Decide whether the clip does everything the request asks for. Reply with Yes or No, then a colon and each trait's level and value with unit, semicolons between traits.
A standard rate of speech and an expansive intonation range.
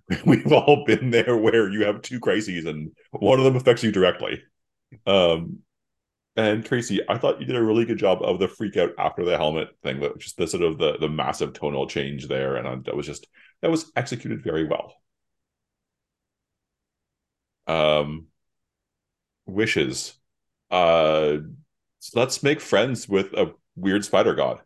Yes: average, 165 wpm; wide, 7.3 semitones